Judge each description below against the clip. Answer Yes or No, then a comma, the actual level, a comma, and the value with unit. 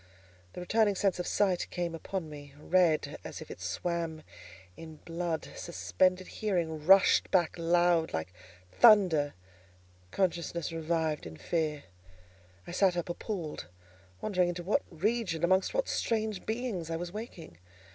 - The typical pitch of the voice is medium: Yes, medium, 175 Hz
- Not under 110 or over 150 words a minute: Yes, slow, 135 wpm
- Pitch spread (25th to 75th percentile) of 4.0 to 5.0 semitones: No, average, 3.0 semitones